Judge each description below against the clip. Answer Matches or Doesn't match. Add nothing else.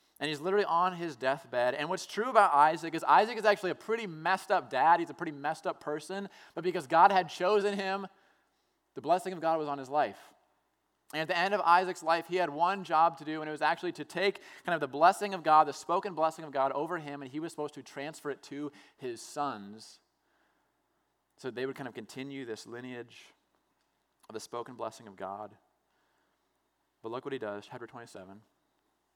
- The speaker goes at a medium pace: Doesn't match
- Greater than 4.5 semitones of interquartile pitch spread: Matches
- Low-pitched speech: Doesn't match